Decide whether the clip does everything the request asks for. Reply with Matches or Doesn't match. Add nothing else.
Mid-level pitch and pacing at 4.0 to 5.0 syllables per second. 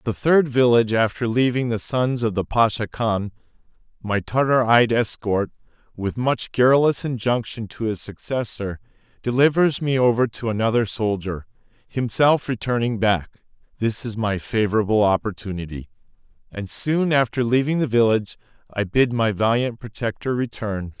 Doesn't match